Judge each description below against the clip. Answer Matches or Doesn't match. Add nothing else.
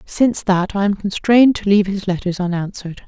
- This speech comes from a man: Doesn't match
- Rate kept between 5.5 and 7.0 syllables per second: Matches